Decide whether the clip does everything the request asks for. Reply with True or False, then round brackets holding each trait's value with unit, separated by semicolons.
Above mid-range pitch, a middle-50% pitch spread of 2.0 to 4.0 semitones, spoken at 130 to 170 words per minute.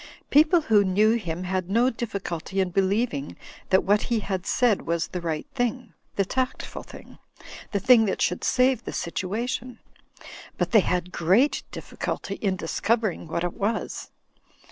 False (200 Hz; 4.8 semitones; 160 wpm)